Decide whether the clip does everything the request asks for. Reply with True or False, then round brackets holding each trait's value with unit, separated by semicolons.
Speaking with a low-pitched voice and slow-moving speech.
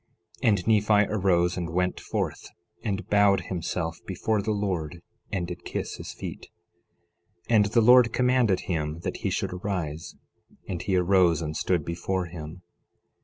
False (90 Hz; 160 wpm)